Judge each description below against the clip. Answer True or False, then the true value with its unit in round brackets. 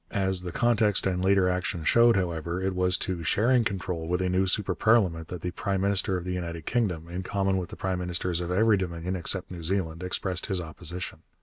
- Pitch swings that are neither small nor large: False (1.8 semitones)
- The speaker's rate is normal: False (215 wpm)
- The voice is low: True (90 Hz)